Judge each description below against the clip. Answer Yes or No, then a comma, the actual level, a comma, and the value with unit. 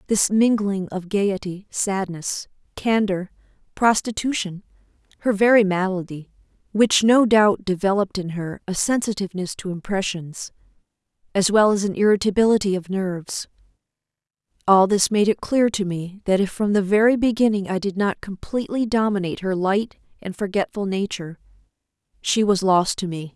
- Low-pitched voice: No, high, 200 Hz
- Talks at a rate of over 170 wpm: No, average, 140 wpm